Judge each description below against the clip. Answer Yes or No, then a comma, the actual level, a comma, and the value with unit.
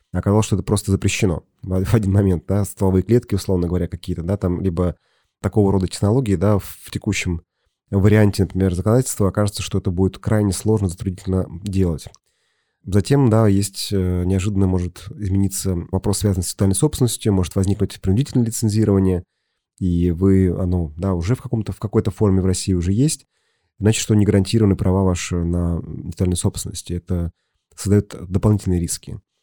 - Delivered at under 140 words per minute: No, average, 155 wpm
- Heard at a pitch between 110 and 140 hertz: No, very low, 95 Hz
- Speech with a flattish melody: Yes, narrow, 2.2 semitones